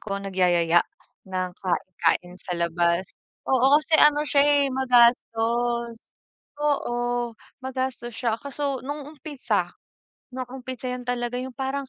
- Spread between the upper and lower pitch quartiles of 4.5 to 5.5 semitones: Yes, average, 5.1 semitones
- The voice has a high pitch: Yes, high, 245 Hz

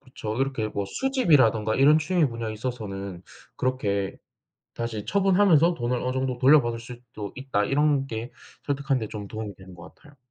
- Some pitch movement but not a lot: Yes, average, 4.7 semitones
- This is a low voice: Yes, low, 125 Hz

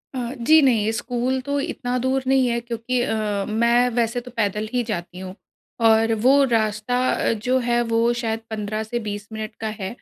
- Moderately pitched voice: No, high, 235 Hz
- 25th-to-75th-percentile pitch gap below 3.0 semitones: Yes, narrow, 2.4 semitones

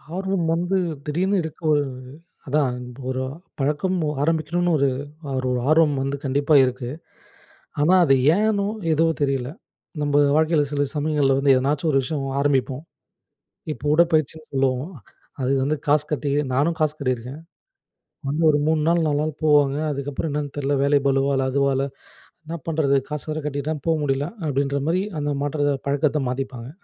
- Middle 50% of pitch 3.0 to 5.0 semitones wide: No, narrow, 2.4 semitones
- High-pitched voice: No, medium, 145 Hz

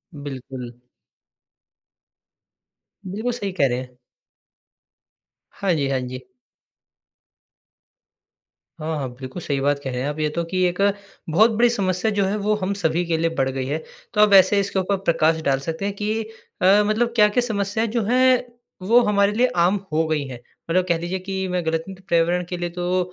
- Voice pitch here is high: No, medium, 180 Hz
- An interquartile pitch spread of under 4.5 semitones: No, average, 4.8 semitones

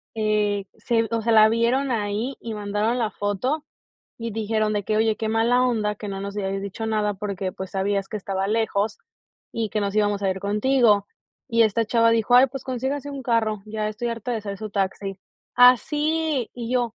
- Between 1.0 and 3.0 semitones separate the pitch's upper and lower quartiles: Yes, narrow, 2.6 semitones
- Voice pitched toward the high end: Yes, high, 220 Hz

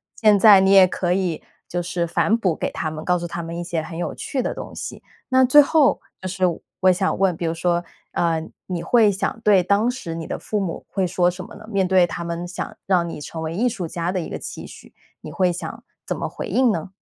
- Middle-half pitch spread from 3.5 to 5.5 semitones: No, average, 2.8 semitones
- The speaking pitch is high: No, medium, 180 Hz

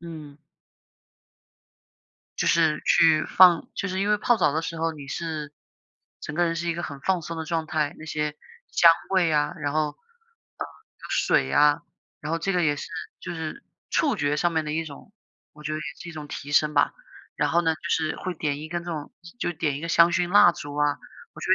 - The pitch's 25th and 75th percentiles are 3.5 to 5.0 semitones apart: No, narrow, 2.4 semitones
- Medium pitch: Yes, medium, 160 Hz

